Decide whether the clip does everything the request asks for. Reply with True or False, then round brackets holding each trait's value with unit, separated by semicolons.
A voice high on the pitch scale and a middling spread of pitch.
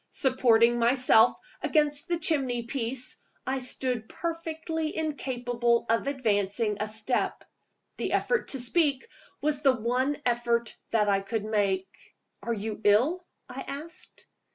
True (245 Hz; 4.2 semitones)